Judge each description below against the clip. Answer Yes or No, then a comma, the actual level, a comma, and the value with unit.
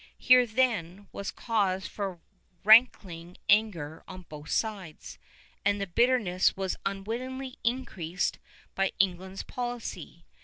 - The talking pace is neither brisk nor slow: No, slow, 110 wpm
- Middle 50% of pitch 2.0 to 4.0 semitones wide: No, average, 4.4 semitones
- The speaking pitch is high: Yes, high, 200 Hz